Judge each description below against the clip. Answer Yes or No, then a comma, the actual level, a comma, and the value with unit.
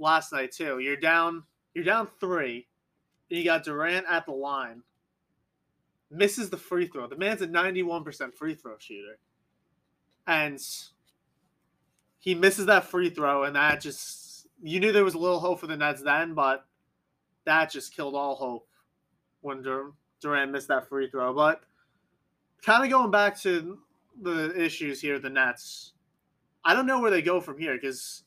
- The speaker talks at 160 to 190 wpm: Yes, average, 170 wpm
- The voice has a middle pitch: Yes, medium, 165 Hz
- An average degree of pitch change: Yes, average, 4.4 semitones